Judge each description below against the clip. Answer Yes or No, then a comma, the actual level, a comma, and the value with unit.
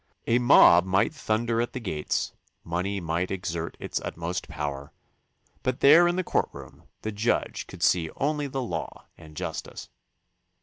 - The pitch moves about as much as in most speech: No, wide, 6.7 semitones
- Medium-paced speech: Yes, average, 150 wpm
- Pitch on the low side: Yes, low, 100 Hz